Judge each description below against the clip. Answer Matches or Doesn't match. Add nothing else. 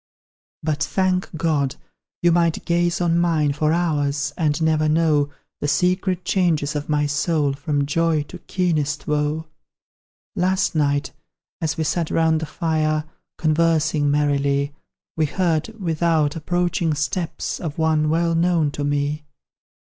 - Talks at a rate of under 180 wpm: Matches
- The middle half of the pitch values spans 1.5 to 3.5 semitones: Matches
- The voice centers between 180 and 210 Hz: Doesn't match